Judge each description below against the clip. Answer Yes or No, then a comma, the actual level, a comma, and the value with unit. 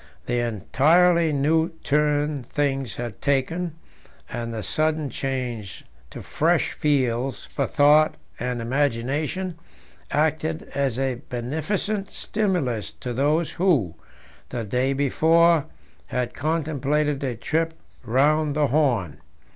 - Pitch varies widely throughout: No, average, 4.1 semitones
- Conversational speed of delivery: No, slow, 110 wpm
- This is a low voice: No, medium, 145 Hz